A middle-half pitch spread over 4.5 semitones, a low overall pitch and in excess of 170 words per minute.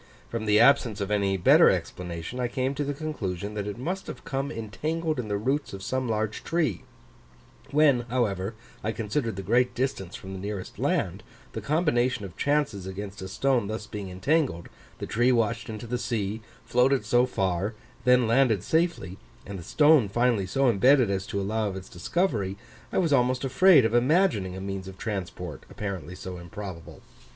Yes: average, 5.1 semitones; low, 110 Hz; average, 180 wpm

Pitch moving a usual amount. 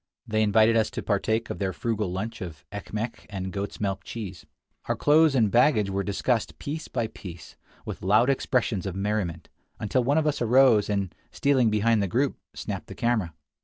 Yes: average, 3.6 semitones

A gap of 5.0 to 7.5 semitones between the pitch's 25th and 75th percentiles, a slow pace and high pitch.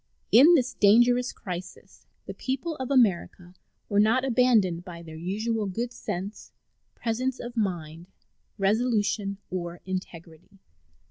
Yes: average, 5.3 semitones; slow, 120 wpm; high, 210 Hz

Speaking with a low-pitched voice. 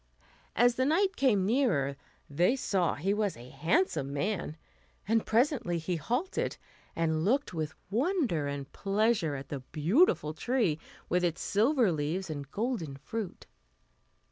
No: high, 190 Hz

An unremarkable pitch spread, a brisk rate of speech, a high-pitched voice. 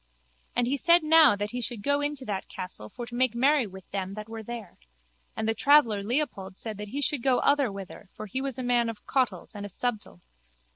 Yes: average, 4.8 semitones; fast, 230 wpm; high, 235 Hz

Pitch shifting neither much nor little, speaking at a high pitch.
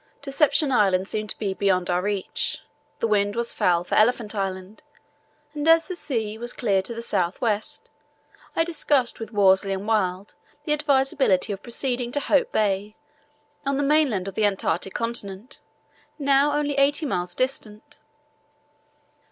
No: wide, 6.0 semitones; high, 220 Hz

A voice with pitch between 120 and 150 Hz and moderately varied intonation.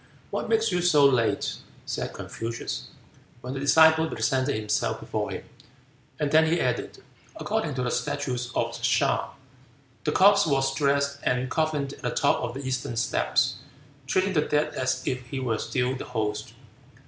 Yes: low, 135 Hz; average, 3.5 semitones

